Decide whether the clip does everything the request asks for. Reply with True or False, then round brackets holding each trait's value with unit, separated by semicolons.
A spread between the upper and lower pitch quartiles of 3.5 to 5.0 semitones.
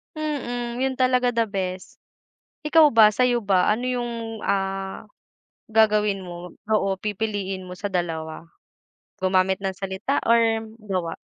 True (4.1 semitones)